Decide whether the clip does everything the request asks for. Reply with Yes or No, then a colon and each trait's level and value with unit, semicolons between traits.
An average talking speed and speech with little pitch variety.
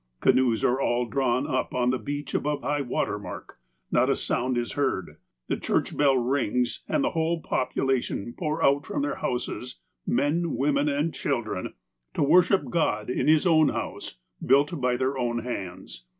No: average, 180 wpm; average, 3.4 semitones